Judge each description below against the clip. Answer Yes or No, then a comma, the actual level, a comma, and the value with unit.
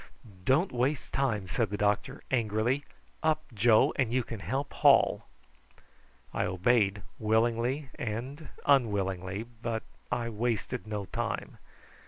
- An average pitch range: Yes, average, 3.8 semitones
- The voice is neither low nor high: No, low, 115 Hz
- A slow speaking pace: Yes, slow, 120 wpm